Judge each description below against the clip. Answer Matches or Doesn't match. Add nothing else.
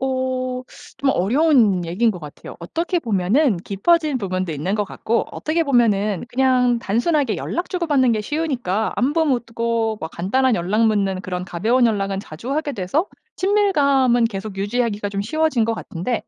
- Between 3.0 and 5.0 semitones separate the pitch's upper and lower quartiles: Doesn't match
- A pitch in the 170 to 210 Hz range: Doesn't match